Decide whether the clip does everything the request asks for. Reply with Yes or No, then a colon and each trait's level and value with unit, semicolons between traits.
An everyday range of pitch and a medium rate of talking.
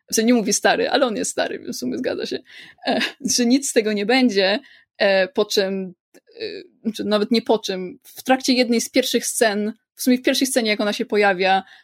No: average, 3.5 semitones; fast, 230 wpm